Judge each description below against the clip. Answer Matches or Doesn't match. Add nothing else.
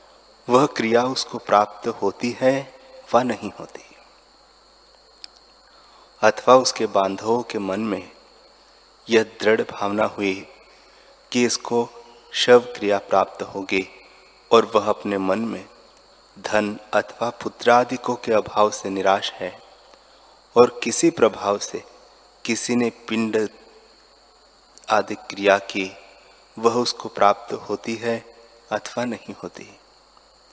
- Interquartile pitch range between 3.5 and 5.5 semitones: Doesn't match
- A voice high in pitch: Doesn't match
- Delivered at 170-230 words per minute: Doesn't match